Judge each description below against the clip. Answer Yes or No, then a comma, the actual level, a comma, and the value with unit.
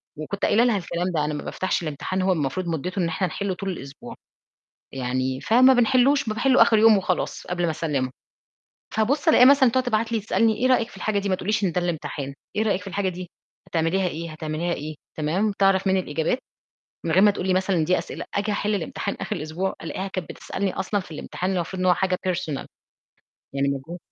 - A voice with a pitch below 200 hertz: Yes, medium, 185 Hz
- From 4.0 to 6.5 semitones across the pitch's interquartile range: Yes, average, 4.4 semitones